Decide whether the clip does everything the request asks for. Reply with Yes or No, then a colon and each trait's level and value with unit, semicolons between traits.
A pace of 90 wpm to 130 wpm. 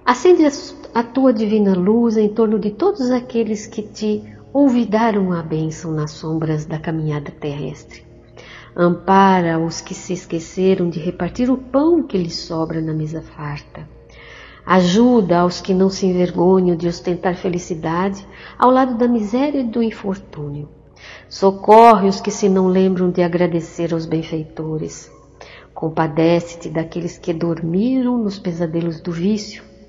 No: average, 140 wpm